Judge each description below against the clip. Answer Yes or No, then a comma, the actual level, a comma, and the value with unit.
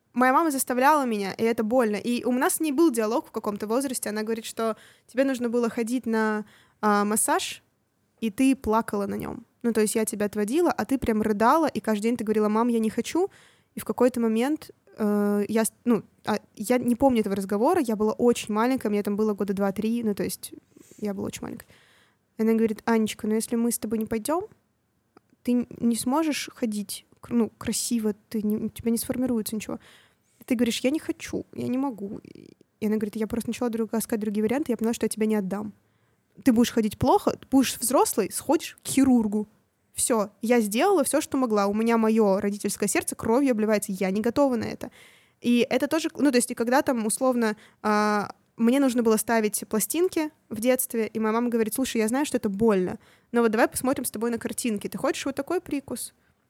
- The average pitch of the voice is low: No, high, 230 Hz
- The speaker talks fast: Yes, fast, 210 wpm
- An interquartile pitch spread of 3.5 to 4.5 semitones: No, average, 3.0 semitones